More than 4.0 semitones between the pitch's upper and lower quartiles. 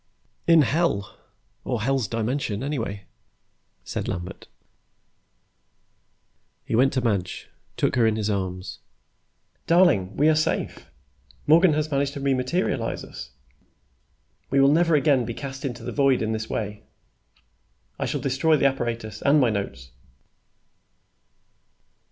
Yes: average, 5.0 semitones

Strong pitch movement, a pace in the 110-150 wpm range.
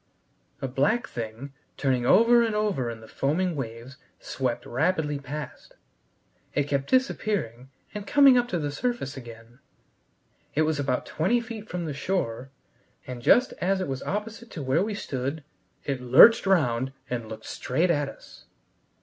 No: wide, 7.9 semitones; average, 160 wpm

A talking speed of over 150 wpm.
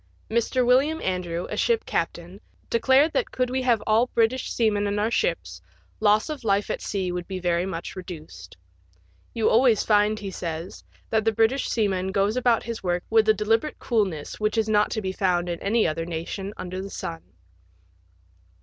Yes: average, 185 wpm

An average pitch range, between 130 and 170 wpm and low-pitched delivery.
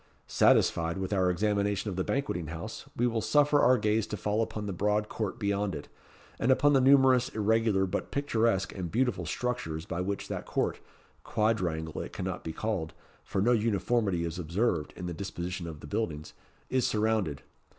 No: average, 4.5 semitones; average, 180 wpm; low, 100 Hz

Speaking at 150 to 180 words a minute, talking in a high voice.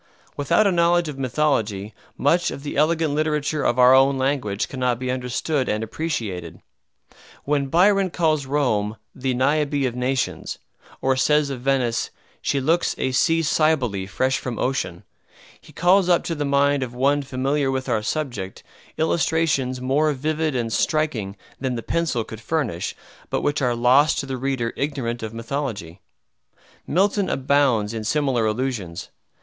No: average, 155 wpm; low, 135 Hz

